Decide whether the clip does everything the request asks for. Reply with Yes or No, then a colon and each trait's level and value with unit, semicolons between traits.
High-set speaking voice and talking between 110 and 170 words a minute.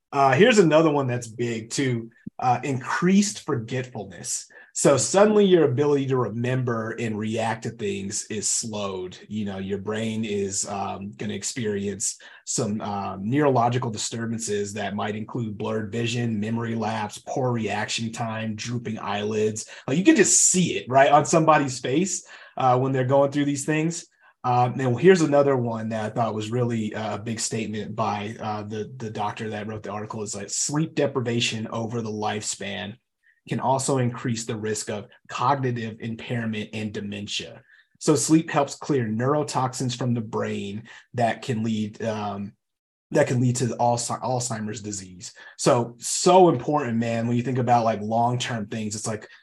No: low, 115 Hz; average, 165 wpm